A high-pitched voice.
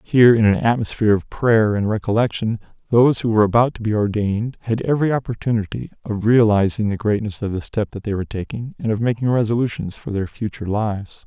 No: low, 110 Hz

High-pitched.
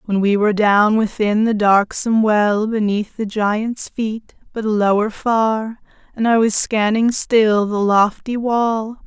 Yes: high, 215 Hz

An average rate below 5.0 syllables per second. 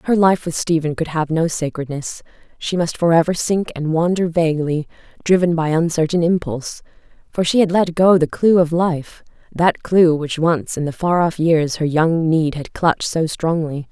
Yes: 4.8 syllables/s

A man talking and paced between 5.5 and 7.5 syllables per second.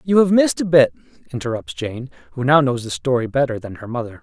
Yes: male; 6.3 syllables/s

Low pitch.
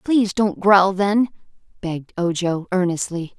No: high, 190 Hz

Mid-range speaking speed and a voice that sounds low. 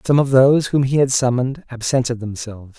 Yes: average, 195 wpm; low, 125 Hz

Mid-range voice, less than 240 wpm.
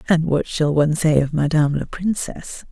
Yes: medium, 155 Hz; average, 200 wpm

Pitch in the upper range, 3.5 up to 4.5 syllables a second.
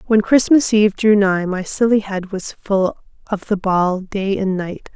Yes: high, 200 Hz; 4.3 syllables/s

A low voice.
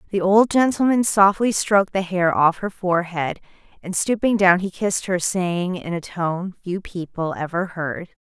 No: medium, 185 Hz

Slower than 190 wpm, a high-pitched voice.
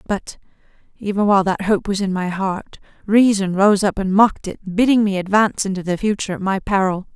No: average, 200 wpm; high, 195 Hz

